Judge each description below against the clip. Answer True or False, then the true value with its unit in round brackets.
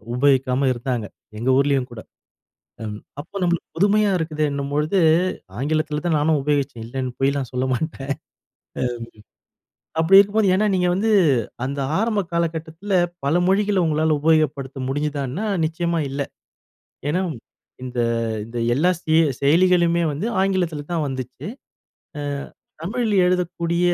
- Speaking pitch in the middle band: True (155 Hz)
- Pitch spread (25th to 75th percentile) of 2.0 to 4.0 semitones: False (4.4 semitones)